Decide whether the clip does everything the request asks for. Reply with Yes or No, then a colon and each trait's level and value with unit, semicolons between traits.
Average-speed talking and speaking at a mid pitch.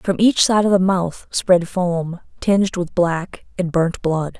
Yes: average, 190 wpm; medium, 180 Hz